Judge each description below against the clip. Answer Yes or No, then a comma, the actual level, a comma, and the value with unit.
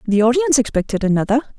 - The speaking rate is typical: Yes, average, 150 wpm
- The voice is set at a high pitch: Yes, high, 240 Hz